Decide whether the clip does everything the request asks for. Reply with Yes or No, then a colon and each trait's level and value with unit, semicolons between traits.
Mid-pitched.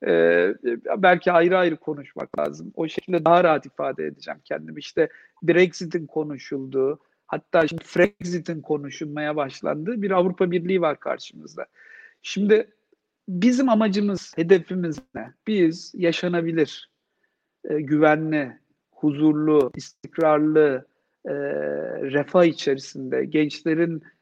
Yes: medium, 160 Hz